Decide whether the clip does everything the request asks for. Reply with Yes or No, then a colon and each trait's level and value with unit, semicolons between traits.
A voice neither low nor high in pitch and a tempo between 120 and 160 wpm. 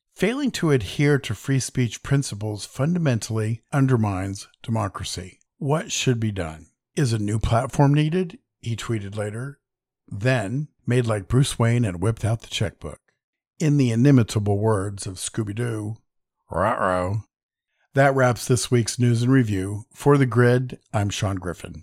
No: low, 115 Hz; average, 145 wpm